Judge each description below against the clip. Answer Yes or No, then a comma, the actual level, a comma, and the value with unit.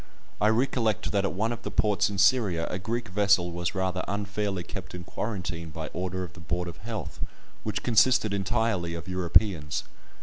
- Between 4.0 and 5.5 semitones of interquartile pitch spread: No, average, 3.3 semitones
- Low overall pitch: Yes, very low, 95 Hz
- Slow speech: No, average, 180 wpm